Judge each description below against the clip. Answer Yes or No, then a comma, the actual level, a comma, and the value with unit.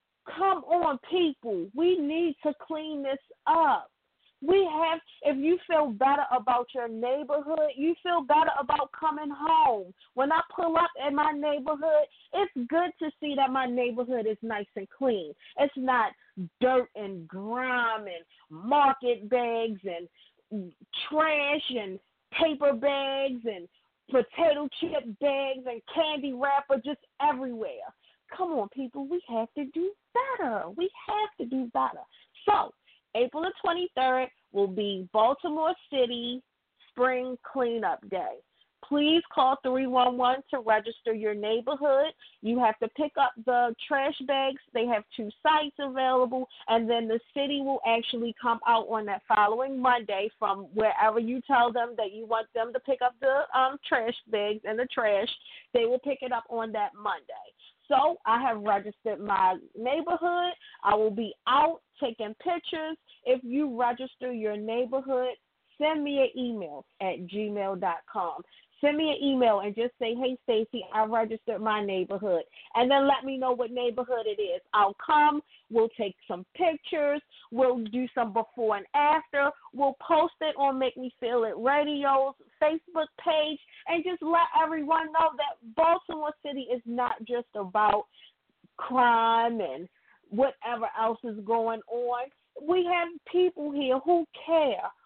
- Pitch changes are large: No, average, 4.9 semitones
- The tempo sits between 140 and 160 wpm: Yes, average, 150 wpm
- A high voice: Yes, very high, 260 Hz